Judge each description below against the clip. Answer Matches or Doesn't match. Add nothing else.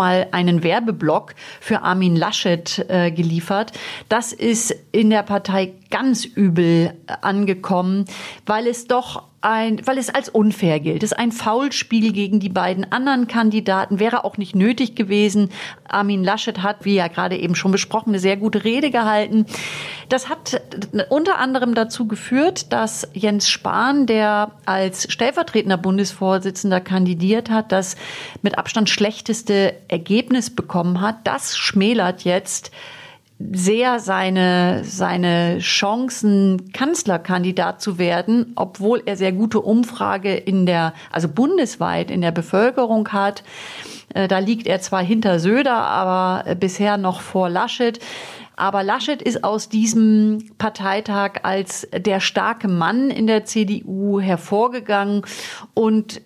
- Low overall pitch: Doesn't match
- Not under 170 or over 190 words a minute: Doesn't match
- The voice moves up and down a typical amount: Matches